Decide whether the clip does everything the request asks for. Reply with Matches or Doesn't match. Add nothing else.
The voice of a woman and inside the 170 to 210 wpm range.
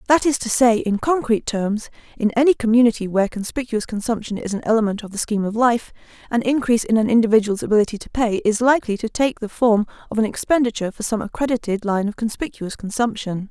Matches